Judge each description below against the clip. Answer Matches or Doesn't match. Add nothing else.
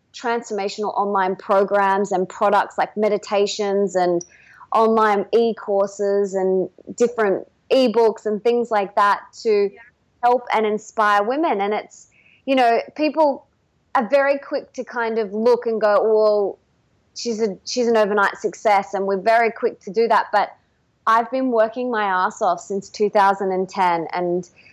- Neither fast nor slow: Matches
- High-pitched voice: Matches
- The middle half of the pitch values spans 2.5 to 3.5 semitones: Matches